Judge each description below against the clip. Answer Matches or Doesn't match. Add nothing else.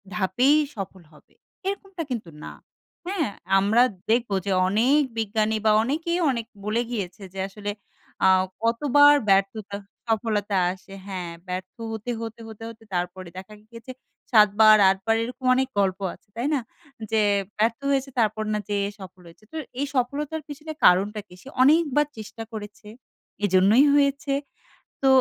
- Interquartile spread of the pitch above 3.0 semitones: Matches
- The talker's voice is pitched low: Doesn't match